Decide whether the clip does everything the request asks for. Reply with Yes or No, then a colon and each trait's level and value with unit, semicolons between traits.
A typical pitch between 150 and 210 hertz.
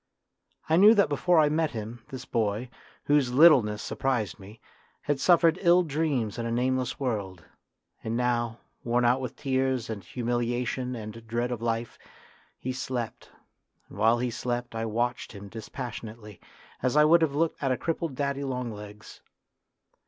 No: low, 125 Hz